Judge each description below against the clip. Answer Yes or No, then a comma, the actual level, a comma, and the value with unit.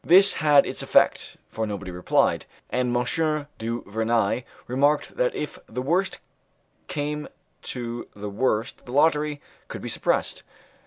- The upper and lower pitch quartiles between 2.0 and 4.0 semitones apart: No, average, 4.9 semitones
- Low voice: Yes, low, 125 Hz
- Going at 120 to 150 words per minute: Yes, average, 140 wpm